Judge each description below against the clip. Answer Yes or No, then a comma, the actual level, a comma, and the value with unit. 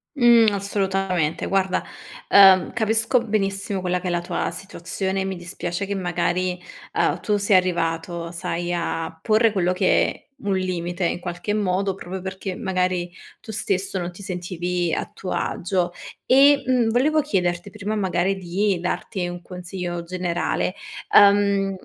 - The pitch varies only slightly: Yes, narrow, 2.2 semitones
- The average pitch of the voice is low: No, medium, 185 Hz